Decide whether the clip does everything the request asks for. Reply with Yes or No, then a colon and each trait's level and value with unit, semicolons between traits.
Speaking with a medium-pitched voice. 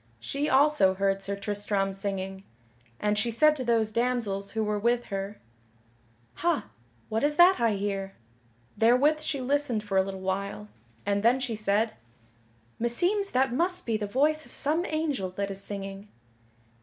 No: high, 220 Hz